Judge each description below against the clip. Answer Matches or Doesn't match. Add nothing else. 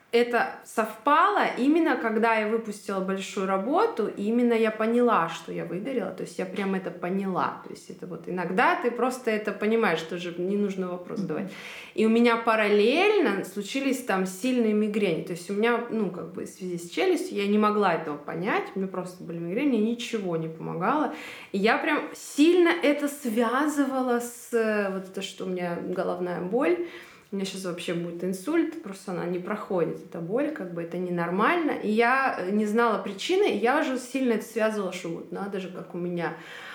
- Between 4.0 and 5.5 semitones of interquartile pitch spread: Matches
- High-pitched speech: Matches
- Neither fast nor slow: Doesn't match